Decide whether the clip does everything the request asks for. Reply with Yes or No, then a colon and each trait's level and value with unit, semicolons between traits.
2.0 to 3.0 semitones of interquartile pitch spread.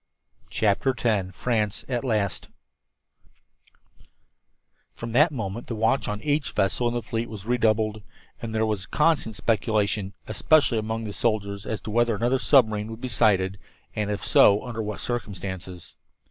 Yes: narrow, 2.6 semitones